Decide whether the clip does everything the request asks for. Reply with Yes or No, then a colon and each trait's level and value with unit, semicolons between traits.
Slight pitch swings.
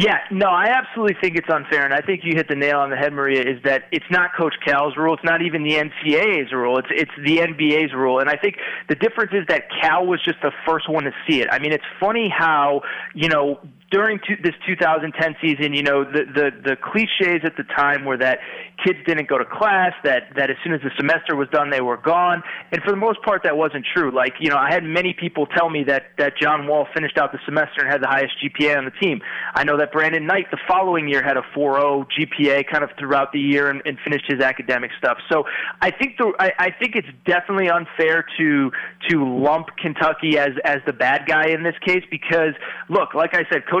No: average, 3.5 semitones